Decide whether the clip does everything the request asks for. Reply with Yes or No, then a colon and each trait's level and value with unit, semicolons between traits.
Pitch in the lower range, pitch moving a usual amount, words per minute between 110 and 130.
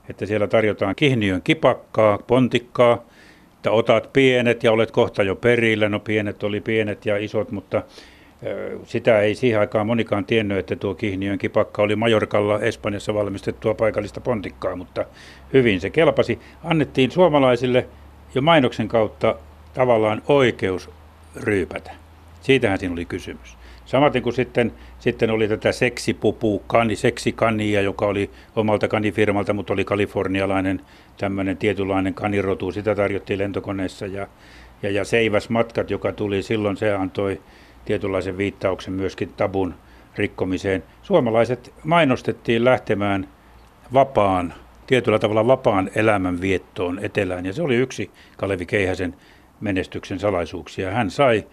Yes: low, 105 Hz; average, 3.0 semitones; average, 125 wpm